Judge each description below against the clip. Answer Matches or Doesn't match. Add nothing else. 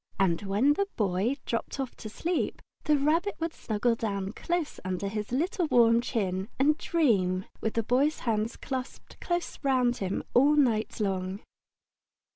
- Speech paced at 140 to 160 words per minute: Matches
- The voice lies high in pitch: Matches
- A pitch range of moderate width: Doesn't match